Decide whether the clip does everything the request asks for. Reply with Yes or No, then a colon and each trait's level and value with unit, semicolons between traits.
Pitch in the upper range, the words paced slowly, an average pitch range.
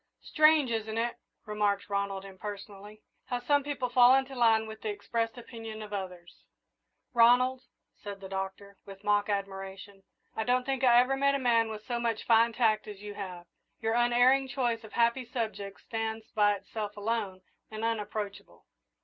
No: high, 220 Hz; average, 165 wpm; average, 3.0 semitones